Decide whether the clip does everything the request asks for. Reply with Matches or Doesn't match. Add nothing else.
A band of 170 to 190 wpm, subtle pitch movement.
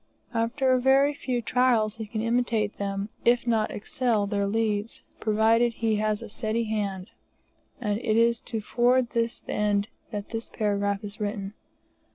Doesn't match